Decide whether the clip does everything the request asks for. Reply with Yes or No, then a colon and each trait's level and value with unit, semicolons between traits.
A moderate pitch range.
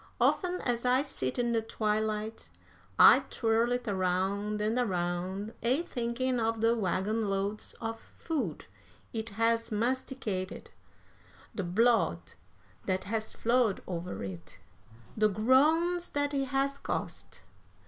Yes: average, 4.0 semitones